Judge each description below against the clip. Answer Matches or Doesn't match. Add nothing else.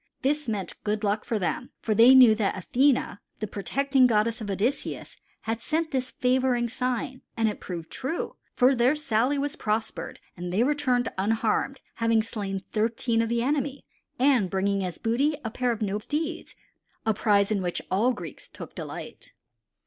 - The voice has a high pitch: Matches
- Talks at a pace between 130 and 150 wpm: Doesn't match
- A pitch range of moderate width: Matches